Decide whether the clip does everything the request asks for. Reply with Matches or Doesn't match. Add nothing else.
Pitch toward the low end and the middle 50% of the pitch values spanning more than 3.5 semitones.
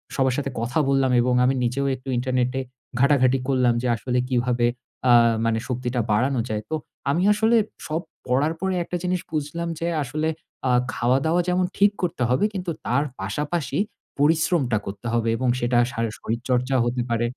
Matches